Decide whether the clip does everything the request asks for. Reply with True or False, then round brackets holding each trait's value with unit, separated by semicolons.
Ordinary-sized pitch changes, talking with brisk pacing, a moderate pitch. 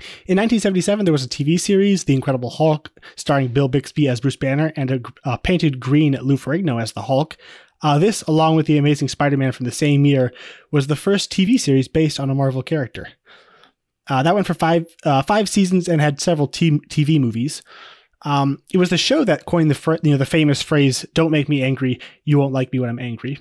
True (3.6 semitones; 220 wpm; 150 Hz)